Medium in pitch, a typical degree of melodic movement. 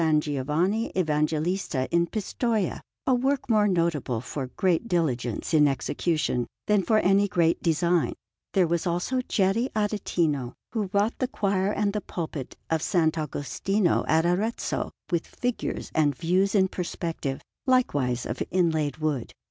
Yes: medium, 175 Hz; average, 4.9 semitones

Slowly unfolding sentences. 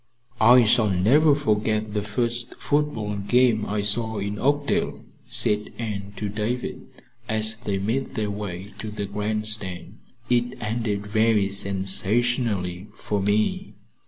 Yes: slow, 130 wpm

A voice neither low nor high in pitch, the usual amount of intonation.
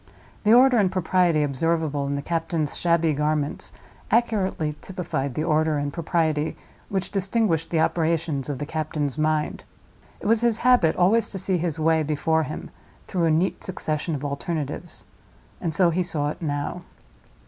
Yes: medium, 160 Hz; average, 3.2 semitones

